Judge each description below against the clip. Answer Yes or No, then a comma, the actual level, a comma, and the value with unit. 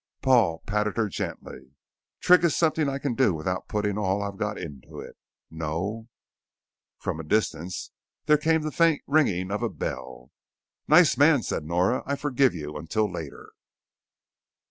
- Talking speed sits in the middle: Yes, average, 160 wpm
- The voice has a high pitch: No, low, 105 Hz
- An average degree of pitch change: No, wide, 8.6 semitones